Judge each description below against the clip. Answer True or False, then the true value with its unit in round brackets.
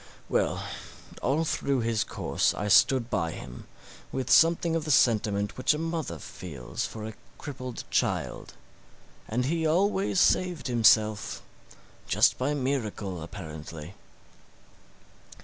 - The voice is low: True (125 Hz)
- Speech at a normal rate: False (120 wpm)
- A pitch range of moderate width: False (7.0 semitones)